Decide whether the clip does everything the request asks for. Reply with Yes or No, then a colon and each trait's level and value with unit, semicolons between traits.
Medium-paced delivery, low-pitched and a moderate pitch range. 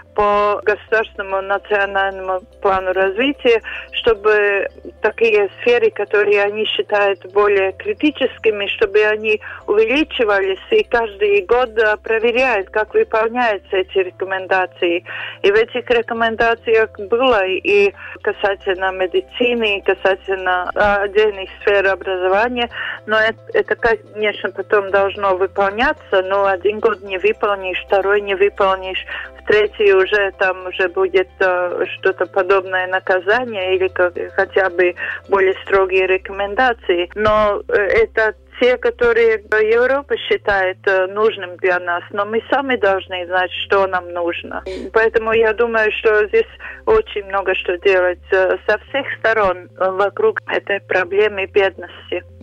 No: average, 120 wpm; high, 205 Hz; average, 3.5 semitones